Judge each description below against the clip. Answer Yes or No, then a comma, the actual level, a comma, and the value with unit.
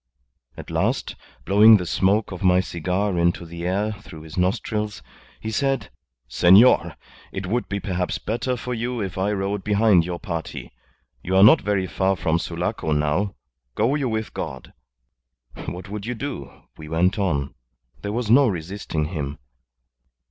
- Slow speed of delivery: No, average, 155 wpm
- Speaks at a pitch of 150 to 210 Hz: No, very low, 95 Hz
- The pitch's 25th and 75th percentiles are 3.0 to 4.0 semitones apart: Yes, average, 3.7 semitones